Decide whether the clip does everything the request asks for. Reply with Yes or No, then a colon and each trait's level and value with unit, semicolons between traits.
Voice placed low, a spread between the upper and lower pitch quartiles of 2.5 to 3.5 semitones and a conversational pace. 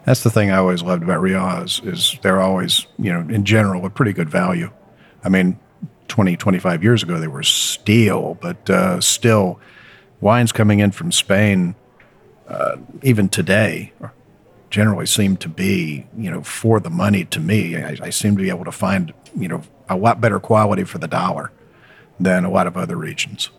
Yes: low, 100 Hz; average, 3.2 semitones; average, 185 wpm